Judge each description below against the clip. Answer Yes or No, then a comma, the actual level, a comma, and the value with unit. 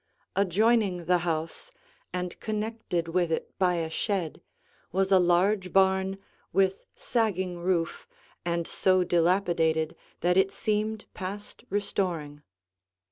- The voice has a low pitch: No, medium, 185 Hz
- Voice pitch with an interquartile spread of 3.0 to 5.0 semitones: No, narrow, 2.5 semitones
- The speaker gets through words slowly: Yes, slow, 115 wpm